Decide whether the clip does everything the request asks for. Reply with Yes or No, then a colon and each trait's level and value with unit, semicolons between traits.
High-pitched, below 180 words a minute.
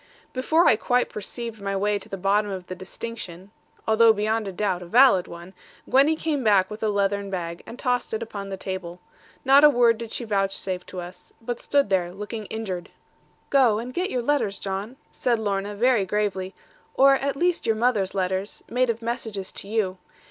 No: high, 210 Hz; average, 190 wpm